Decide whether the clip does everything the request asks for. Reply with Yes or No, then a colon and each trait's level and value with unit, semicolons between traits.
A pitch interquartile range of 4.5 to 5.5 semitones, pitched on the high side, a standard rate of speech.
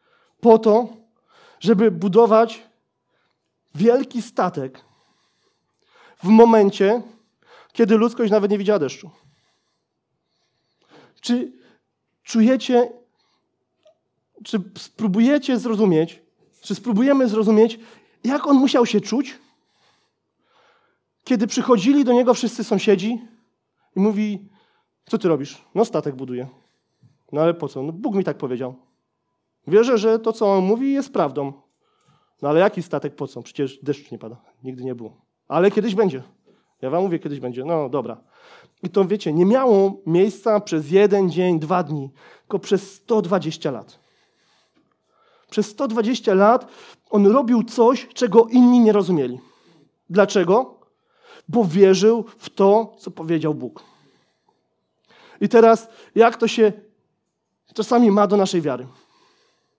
Yes: average, 5.2 semitones; high, 210 Hz; average, 125 wpm